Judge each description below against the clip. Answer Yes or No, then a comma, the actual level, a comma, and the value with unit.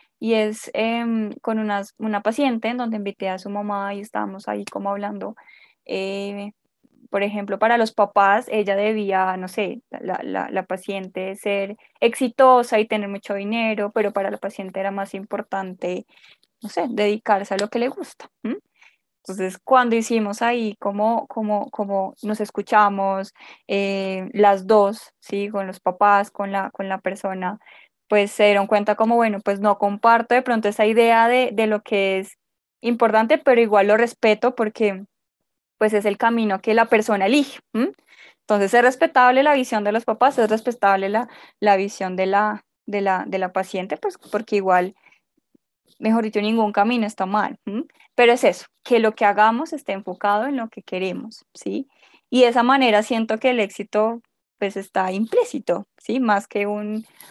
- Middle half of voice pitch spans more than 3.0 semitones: No, narrow, 2.6 semitones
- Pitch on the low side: No, high, 210 Hz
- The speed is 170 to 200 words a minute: Yes, average, 175 wpm